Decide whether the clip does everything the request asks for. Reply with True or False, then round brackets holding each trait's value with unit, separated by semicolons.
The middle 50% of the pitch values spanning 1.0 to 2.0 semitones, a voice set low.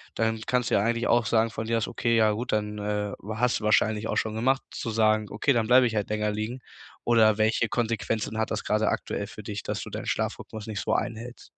True (1.5 semitones; 110 Hz)